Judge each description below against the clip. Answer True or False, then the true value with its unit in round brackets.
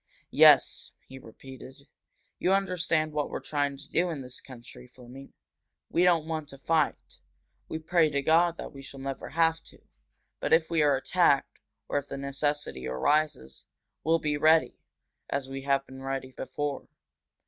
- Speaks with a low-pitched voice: False (145 Hz)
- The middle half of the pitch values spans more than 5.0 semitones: False (3.0 semitones)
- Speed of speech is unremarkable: True (165 wpm)